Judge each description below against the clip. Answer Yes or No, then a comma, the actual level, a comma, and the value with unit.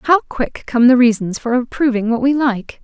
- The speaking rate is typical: No, fast, 210 wpm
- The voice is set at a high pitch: Yes, high, 245 Hz